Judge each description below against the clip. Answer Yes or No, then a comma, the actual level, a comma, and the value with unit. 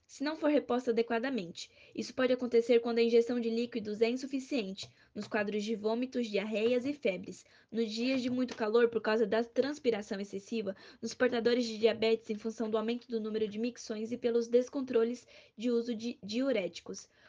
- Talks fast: No, average, 175 wpm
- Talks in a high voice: Yes, high, 235 Hz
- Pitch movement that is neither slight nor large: No, narrow, 1.7 semitones